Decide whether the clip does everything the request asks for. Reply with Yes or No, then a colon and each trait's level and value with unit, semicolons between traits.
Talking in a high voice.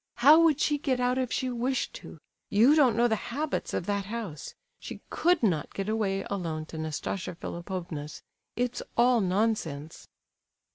Yes: high, 220 Hz